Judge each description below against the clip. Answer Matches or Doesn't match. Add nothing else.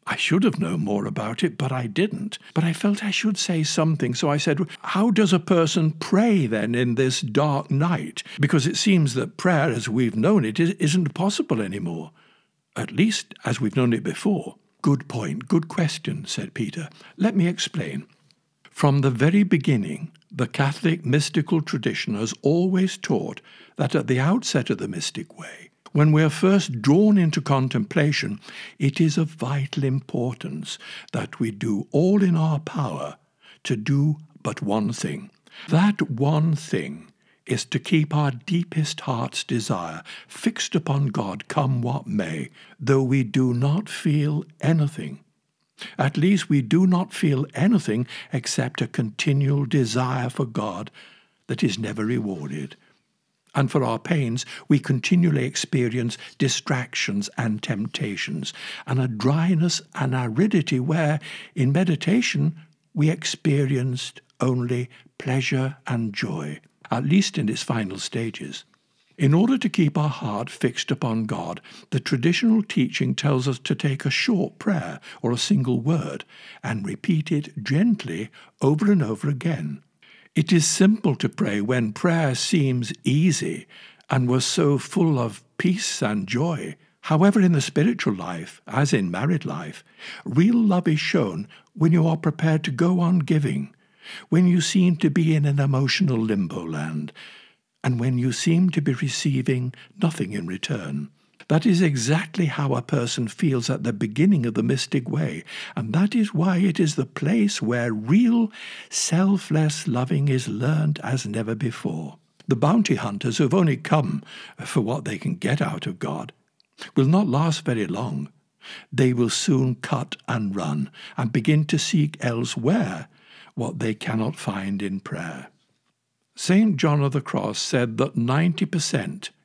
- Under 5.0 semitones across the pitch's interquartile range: Doesn't match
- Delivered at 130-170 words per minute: Matches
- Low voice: Doesn't match